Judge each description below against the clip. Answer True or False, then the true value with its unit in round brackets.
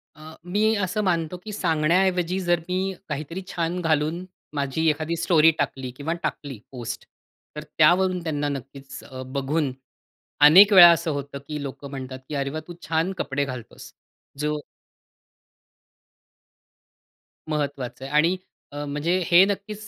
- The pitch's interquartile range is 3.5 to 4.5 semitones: True (3.8 semitones)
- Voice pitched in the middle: True (155 Hz)